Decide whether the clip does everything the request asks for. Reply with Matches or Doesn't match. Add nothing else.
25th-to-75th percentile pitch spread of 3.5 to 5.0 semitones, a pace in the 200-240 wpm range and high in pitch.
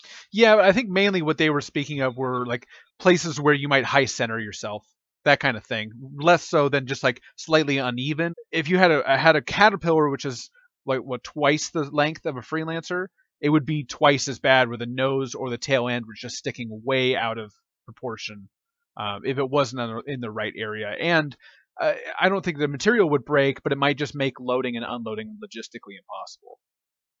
Doesn't match